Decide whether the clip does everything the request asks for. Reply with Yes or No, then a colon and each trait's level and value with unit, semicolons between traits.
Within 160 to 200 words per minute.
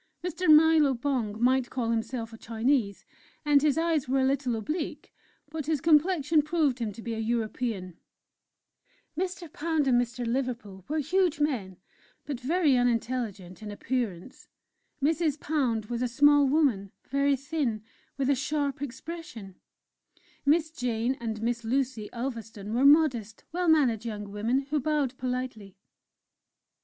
No: average, 145 wpm